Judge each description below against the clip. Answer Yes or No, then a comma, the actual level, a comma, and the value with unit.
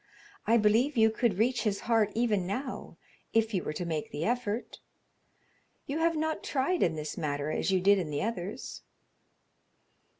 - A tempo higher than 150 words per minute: Yes, average, 170 wpm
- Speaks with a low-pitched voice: No, high, 215 Hz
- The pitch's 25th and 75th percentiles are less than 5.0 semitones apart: No, average, 5.3 semitones